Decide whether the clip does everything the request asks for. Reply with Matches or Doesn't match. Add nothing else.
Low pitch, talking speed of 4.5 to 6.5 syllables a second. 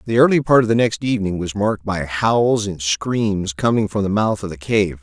Matches